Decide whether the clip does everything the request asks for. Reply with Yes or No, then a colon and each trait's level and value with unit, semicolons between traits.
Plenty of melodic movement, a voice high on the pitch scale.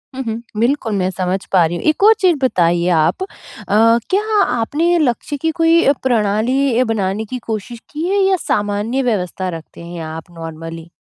Yes: wide, 6.8 semitones; high, 225 Hz